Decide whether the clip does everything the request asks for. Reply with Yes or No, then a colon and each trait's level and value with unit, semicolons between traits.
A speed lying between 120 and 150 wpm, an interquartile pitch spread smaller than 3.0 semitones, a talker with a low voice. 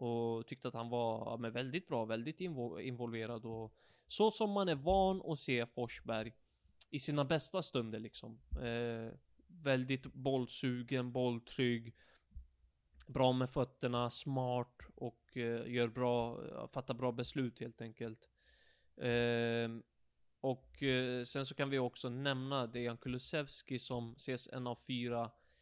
Yes: average, 135 wpm; narrow, 2.4 semitones; low, 125 Hz